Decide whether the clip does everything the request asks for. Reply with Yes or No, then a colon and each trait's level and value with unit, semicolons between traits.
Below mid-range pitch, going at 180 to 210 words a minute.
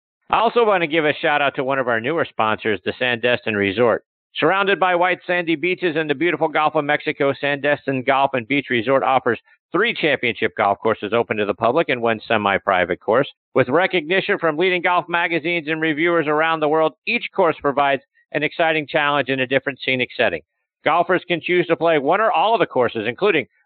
No: medium, 150 Hz; fast, 205 wpm